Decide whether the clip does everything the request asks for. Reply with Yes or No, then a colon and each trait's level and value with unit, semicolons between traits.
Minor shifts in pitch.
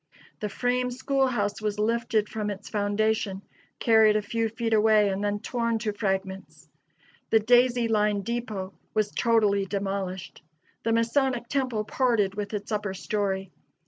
Yes: narrow, 2.3 semitones